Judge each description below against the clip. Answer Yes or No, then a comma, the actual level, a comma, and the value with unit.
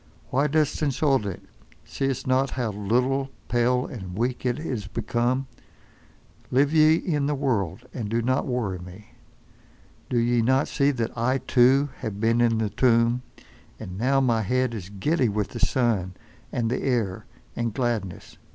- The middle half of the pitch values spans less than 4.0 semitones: Yes, average, 3.2 semitones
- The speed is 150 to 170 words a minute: Yes, average, 155 wpm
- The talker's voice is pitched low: Yes, low, 120 Hz